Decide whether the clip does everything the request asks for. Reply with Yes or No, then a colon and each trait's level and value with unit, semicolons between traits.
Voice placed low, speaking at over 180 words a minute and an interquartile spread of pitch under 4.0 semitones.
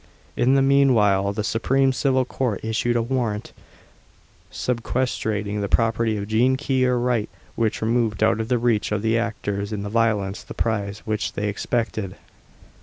No: low, 115 Hz; average, 165 wpm; average, 3.0 semitones